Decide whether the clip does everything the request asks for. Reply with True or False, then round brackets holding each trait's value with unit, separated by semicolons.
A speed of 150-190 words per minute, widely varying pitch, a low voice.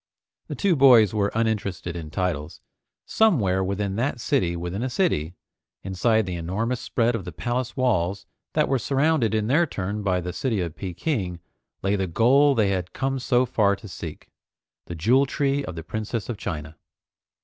True (175 wpm; 5.7 semitones; 105 Hz)